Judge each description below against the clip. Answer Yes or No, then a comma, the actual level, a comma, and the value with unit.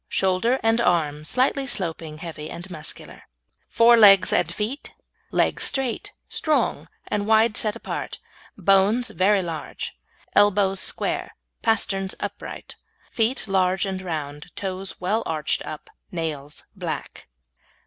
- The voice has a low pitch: No, high, 195 Hz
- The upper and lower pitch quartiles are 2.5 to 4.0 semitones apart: No, average, 4.8 semitones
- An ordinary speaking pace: No, slow, 120 wpm